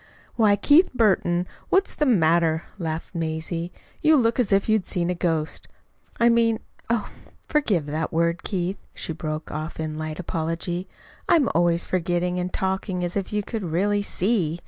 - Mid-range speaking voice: Yes, medium, 180 Hz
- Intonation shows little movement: No, average, 4.2 semitones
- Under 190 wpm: Yes, average, 165 wpm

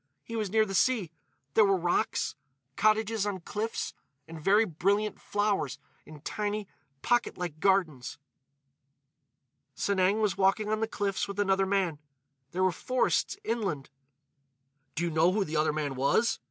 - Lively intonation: No, average, 4.8 semitones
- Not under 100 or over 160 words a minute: Yes, average, 140 wpm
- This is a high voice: Yes, high, 195 Hz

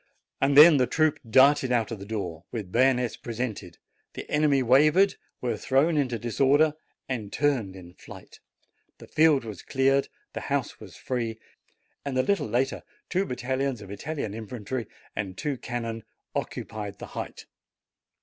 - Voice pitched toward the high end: No, low, 125 Hz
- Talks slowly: No, average, 150 wpm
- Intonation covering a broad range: No, average, 4.1 semitones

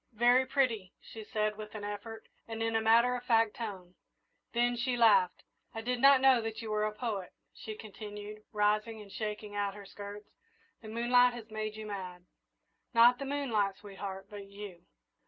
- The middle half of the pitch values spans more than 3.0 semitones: No, narrow, 2.4 semitones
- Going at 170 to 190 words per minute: Yes, average, 175 wpm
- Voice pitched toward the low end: No, high, 215 Hz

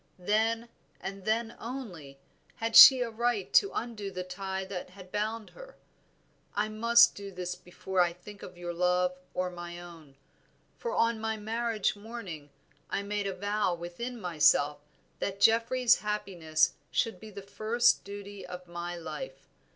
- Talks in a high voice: Yes, high, 200 Hz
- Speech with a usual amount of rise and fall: Yes, average, 4.1 semitones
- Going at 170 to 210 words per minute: No, average, 155 wpm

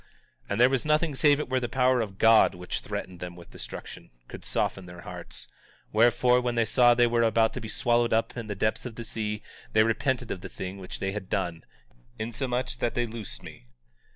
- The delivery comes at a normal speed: No, fast, 225 wpm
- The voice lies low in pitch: Yes, low, 115 Hz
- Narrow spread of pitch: No, average, 3.3 semitones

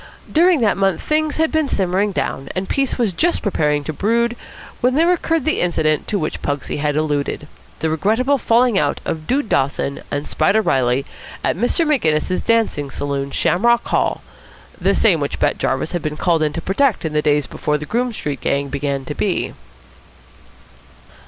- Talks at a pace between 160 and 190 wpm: Yes, average, 180 wpm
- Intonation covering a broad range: Yes, wide, 8.4 semitones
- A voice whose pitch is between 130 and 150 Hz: No, medium, 180 Hz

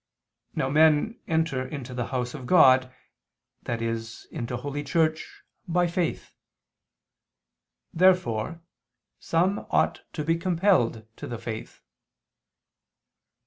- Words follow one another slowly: Yes, slow, 100 wpm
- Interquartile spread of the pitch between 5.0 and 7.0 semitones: Yes, average, 5.3 semitones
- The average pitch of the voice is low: No, medium, 145 Hz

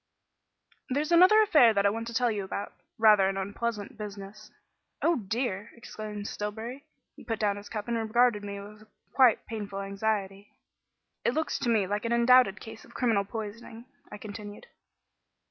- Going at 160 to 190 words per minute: Yes, average, 165 wpm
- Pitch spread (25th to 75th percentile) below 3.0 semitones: Yes, narrow, 2.6 semitones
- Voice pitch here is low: No, high, 215 Hz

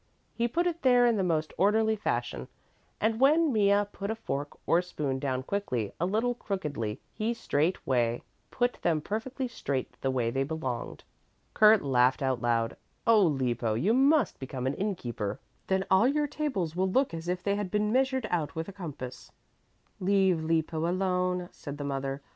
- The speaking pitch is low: No, medium, 180 Hz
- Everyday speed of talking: Yes, average, 175 wpm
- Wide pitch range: Yes, wide, 8.1 semitones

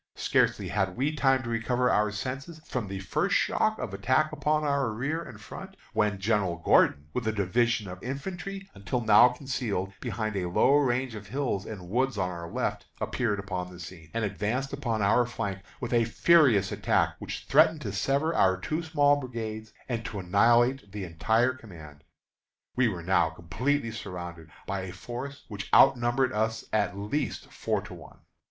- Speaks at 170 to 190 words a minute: Yes, average, 175 wpm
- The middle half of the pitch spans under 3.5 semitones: No, average, 5.3 semitones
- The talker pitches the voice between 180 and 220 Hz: No, low, 115 Hz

